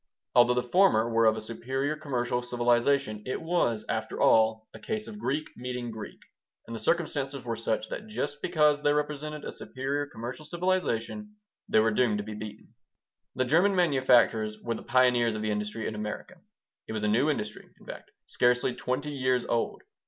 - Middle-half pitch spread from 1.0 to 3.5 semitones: No, average, 4.7 semitones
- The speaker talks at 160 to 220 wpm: Yes, average, 180 wpm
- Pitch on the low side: Yes, low, 125 Hz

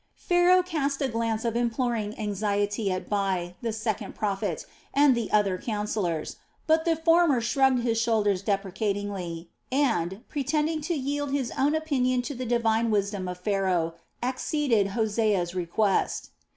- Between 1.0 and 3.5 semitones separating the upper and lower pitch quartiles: No, average, 5.3 semitones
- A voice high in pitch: Yes, high, 225 Hz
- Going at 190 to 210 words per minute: No, average, 145 wpm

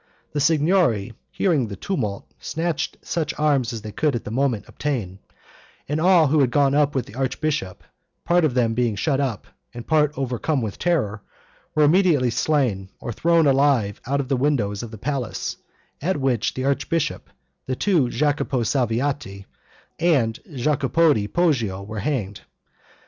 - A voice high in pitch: No, low, 135 Hz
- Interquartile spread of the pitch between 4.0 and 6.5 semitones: Yes, average, 4.9 semitones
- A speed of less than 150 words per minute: No, average, 160 wpm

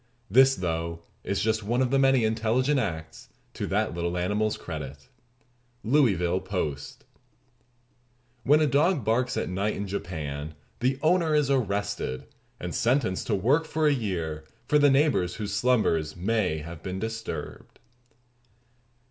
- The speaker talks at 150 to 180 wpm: No, average, 140 wpm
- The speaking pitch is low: Yes, low, 105 Hz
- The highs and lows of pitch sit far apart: Yes, wide, 7.1 semitones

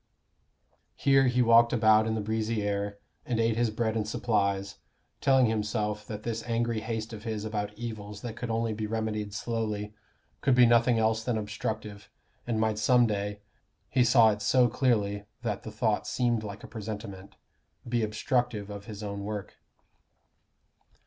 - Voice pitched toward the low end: Yes, low, 110 Hz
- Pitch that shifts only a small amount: Yes, narrow, 2.0 semitones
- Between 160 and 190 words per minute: Yes, average, 165 wpm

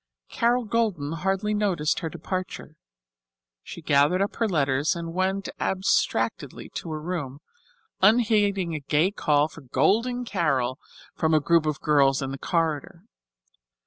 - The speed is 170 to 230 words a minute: No, average, 140 wpm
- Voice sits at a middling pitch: Yes, medium, 170 Hz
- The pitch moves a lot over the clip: No, average, 4.9 semitones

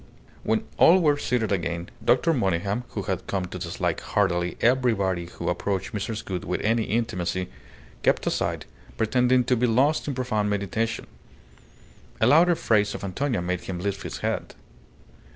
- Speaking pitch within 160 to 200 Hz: No, low, 105 Hz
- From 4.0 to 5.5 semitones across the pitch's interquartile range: Yes, average, 5.1 semitones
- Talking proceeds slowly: No, average, 155 wpm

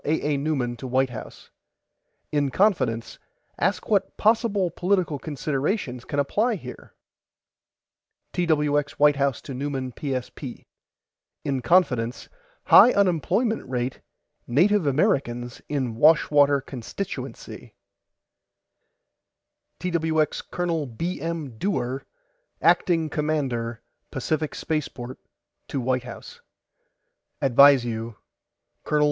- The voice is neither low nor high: Yes, medium, 145 Hz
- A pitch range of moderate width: Yes, average, 4.7 semitones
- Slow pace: Yes, slow, 95 wpm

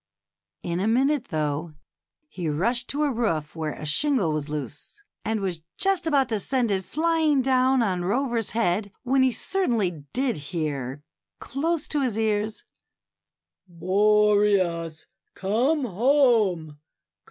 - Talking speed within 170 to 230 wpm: No, slow, 135 wpm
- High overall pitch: Yes, high, 210 Hz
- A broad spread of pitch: Yes, wide, 7.5 semitones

